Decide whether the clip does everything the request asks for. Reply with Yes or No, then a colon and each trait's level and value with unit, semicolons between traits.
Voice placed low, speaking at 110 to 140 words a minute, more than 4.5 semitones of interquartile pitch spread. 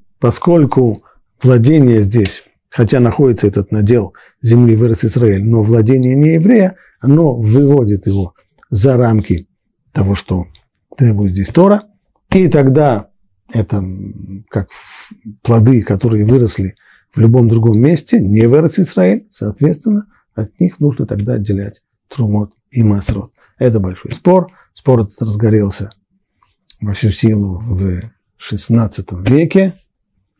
Yes: low, 115 Hz; average, 115 wpm; average, 4.9 semitones